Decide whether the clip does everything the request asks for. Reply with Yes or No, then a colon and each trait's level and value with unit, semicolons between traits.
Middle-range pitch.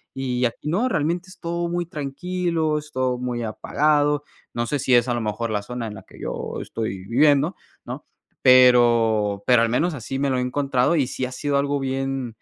No: low, 130 Hz